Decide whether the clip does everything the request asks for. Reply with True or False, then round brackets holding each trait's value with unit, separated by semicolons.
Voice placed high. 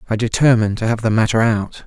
False (115 Hz)